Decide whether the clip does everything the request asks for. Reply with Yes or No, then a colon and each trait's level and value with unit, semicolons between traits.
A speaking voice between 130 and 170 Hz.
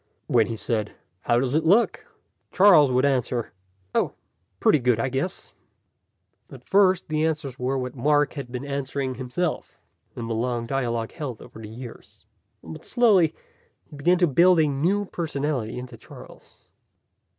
Yes: low, 135 Hz